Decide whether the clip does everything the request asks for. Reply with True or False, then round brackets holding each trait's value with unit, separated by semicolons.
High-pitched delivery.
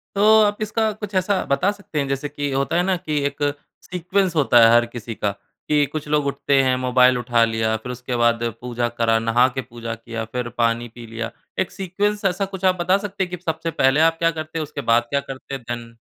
False (140 Hz)